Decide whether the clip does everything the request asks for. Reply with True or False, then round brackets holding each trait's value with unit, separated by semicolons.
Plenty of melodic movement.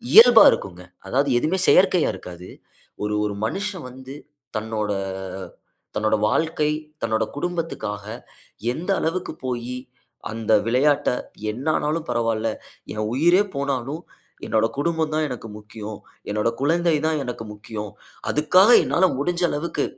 True (6.9 semitones)